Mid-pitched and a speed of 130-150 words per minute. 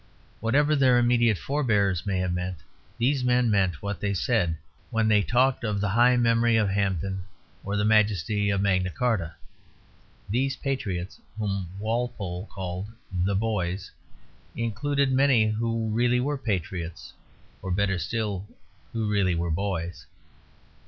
No: low, 105 Hz; average, 140 wpm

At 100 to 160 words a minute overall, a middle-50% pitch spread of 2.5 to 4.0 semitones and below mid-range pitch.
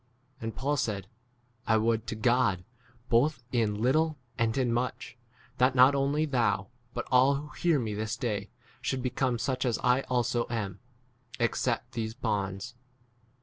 Yes: average, 155 wpm; average, 3.1 semitones; low, 120 Hz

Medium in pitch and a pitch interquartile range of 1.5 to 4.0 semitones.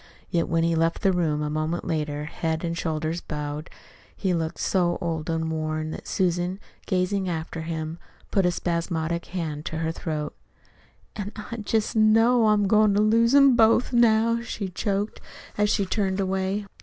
No: medium, 175 Hz; average, 4.4 semitones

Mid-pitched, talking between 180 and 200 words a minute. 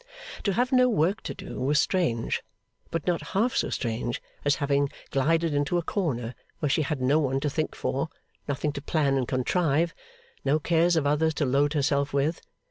Yes: medium, 150 Hz; average, 190 wpm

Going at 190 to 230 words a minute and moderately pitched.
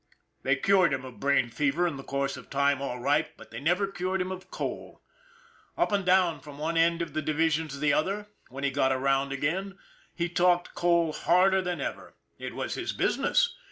Yes: fast, 205 wpm; medium, 160 Hz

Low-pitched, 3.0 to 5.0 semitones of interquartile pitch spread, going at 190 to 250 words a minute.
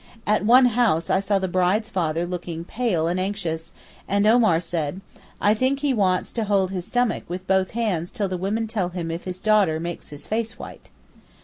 No: high, 190 Hz; average, 3.9 semitones; average, 200 wpm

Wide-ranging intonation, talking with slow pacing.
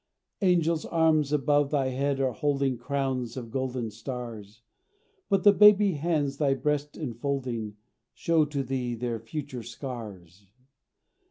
No: average, 3.7 semitones; slow, 125 wpm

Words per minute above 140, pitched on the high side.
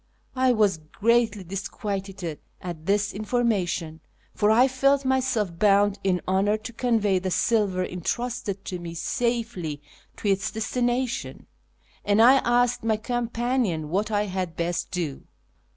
No: slow, 135 wpm; high, 205 Hz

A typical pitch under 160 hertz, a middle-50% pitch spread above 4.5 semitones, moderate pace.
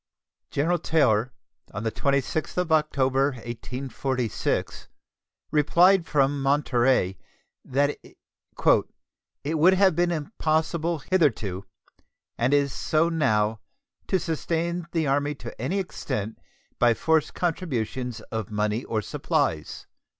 No: medium, 140 Hz; wide, 5.4 semitones; slow, 105 wpm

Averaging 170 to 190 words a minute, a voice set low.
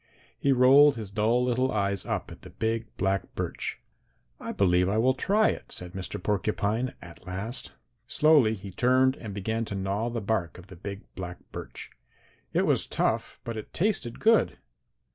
Yes: average, 175 wpm; low, 110 Hz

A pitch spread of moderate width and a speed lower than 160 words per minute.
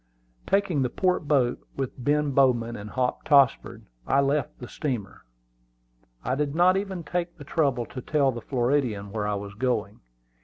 No: average, 3.9 semitones; average, 165 wpm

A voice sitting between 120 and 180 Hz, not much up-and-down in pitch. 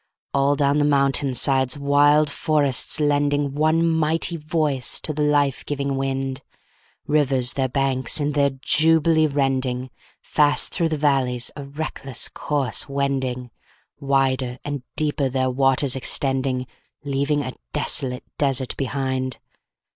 Yes: medium, 140 Hz; narrow, 1.8 semitones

